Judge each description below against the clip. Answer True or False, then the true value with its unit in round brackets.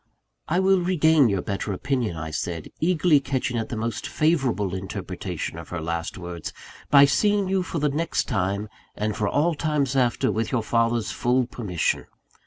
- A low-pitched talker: True (120 Hz)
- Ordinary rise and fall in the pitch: False (7.4 semitones)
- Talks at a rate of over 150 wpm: True (175 wpm)